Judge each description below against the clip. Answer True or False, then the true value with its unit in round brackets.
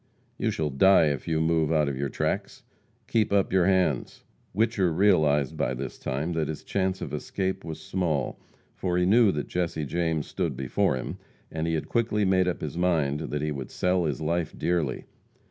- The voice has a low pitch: True (80 Hz)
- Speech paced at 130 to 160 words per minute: False (195 wpm)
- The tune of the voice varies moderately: True (3.9 semitones)